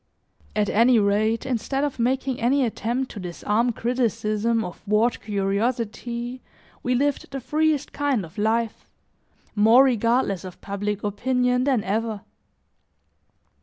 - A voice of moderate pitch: No, high, 230 Hz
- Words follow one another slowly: Yes, slow, 125 wpm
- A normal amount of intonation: Yes, average, 3.4 semitones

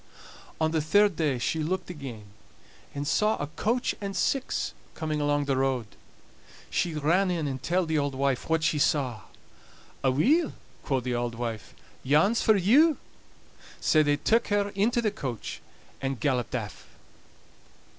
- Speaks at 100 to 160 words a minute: Yes, average, 155 wpm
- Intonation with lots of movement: Yes, wide, 6.6 semitones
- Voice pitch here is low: No, medium, 155 Hz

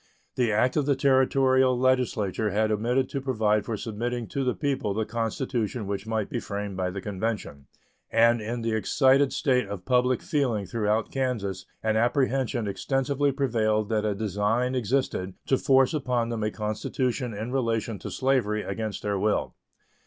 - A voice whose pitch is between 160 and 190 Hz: No, low, 115 Hz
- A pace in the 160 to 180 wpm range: Yes, average, 165 wpm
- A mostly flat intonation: No, average, 3.6 semitones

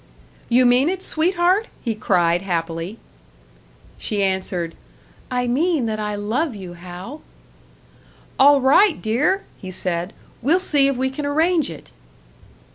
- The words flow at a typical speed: No, slow, 130 wpm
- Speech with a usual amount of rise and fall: No, wide, 8.1 semitones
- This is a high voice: Yes, high, 245 Hz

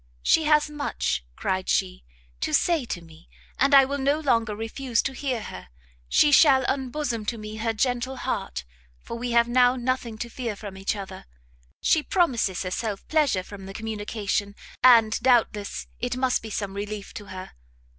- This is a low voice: No, high, 230 Hz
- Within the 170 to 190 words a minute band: Yes, average, 175 wpm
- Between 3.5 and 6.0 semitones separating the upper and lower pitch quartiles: Yes, average, 4.5 semitones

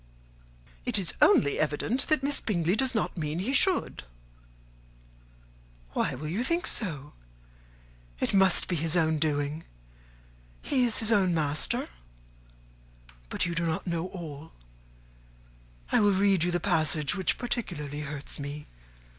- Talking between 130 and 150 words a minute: Yes, average, 140 wpm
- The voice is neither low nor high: Yes, medium, 170 Hz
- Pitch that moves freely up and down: Yes, wide, 5.7 semitones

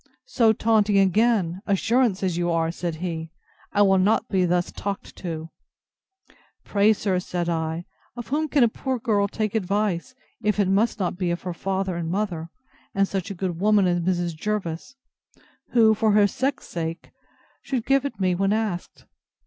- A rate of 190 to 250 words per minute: No, average, 175 wpm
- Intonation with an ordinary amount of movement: Yes, average, 3.8 semitones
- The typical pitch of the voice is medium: No, high, 195 Hz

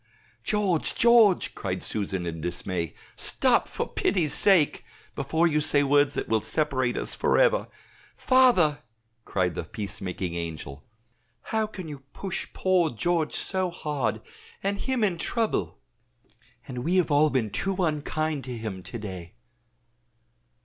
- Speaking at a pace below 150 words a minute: Yes, average, 140 wpm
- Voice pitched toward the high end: No, medium, 150 Hz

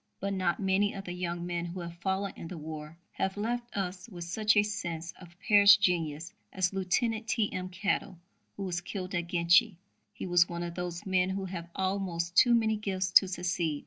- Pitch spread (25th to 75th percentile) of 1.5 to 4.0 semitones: Yes, narrow, 2.4 semitones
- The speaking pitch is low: No, medium, 185 Hz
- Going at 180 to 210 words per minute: Yes, average, 200 wpm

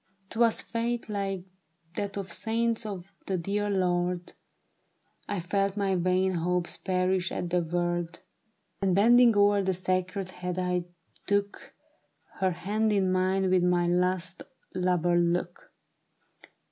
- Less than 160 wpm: Yes, slow, 135 wpm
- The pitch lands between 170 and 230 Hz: Yes, medium, 185 Hz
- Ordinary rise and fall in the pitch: No, narrow, 2.2 semitones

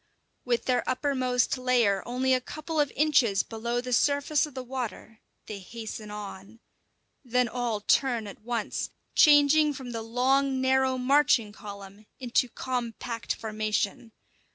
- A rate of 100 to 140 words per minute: Yes, slow, 135 wpm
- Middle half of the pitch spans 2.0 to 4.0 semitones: Yes, average, 3.0 semitones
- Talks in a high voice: Yes, high, 245 Hz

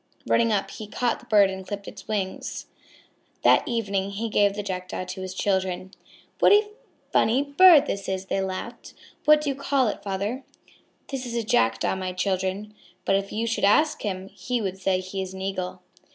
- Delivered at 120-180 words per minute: No, average, 195 wpm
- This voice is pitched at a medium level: No, high, 200 Hz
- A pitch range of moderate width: Yes, average, 3.6 semitones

